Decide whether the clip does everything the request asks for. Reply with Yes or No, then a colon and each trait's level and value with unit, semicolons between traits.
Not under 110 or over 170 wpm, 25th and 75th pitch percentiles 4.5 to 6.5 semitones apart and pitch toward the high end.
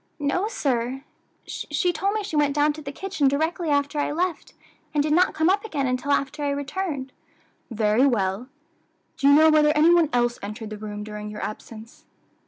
No: average, 190 wpm; average, 4.9 semitones; very high, 285 Hz